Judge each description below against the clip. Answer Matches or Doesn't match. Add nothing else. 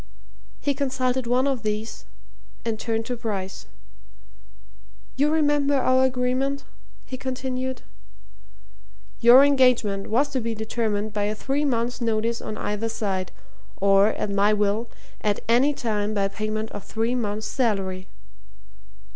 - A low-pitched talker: Doesn't match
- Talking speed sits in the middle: Doesn't match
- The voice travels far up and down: Doesn't match